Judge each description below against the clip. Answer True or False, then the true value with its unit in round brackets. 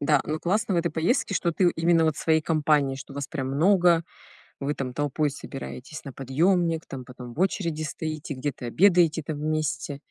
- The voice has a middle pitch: True (155 Hz)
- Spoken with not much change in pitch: False (3.4 semitones)